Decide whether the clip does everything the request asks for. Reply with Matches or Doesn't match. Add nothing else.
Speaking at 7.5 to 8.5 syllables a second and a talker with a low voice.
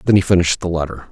Matches